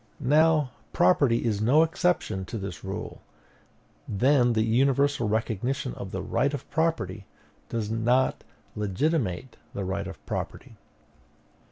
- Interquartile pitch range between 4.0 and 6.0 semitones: Yes, wide, 5.4 semitones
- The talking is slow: Yes, slow, 125 wpm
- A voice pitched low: Yes, low, 115 Hz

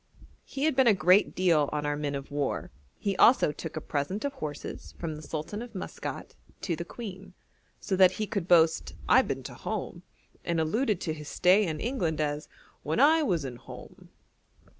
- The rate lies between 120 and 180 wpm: No, average, 195 wpm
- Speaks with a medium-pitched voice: Yes, medium, 170 Hz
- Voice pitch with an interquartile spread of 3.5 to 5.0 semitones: No, wide, 5.4 semitones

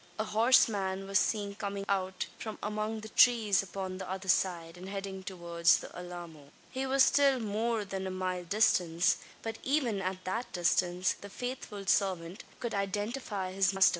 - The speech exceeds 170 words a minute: No, average, 165 wpm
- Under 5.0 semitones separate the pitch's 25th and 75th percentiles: Yes, average, 2.8 semitones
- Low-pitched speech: No, high, 195 Hz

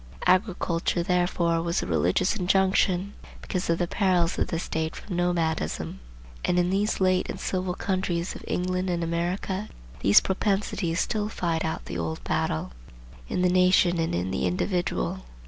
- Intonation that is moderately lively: No, narrow, 2.0 semitones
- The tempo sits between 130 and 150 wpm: No, average, 160 wpm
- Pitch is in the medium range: Yes, medium, 180 Hz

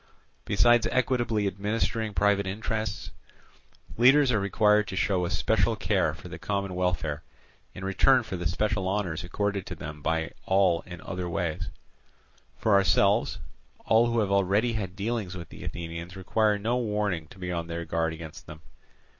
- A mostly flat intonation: No, average, 3.5 semitones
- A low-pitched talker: Yes, low, 100 Hz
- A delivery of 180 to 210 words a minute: No, average, 165 wpm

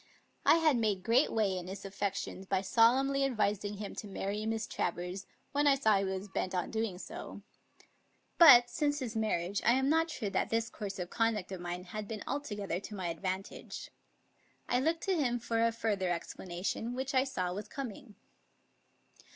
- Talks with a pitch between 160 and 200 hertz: No, high, 215 Hz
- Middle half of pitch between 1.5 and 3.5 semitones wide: No, average, 4.4 semitones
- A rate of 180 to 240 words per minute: Yes, average, 190 wpm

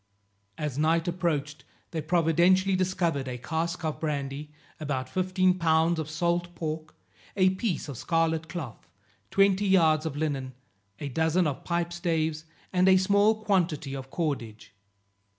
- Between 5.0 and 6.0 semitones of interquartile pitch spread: No, average, 3.3 semitones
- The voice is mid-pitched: Yes, medium, 165 Hz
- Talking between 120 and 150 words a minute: Yes, average, 140 wpm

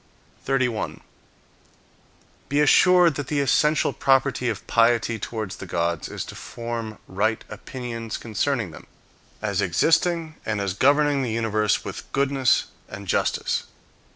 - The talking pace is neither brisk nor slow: No, slow, 130 wpm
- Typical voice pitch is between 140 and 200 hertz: No, low, 120 Hz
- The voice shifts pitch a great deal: No, average, 4.6 semitones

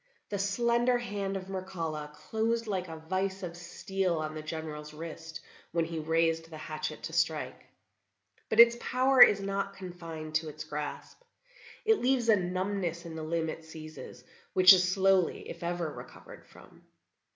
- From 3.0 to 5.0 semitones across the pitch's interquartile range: Yes, average, 3.6 semitones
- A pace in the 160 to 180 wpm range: Yes, average, 165 wpm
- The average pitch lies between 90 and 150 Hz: No, medium, 175 Hz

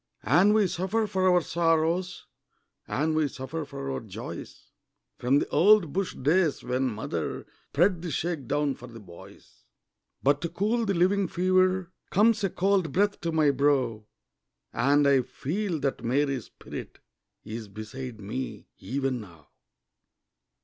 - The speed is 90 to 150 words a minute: Yes, average, 145 wpm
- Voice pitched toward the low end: No, medium, 155 Hz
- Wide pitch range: Yes, wide, 6.0 semitones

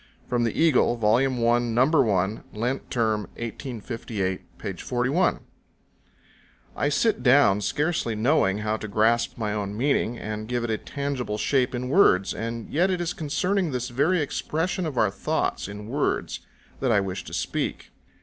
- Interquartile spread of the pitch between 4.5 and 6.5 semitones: Yes, average, 4.9 semitones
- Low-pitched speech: Yes, low, 120 Hz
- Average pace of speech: Yes, average, 160 wpm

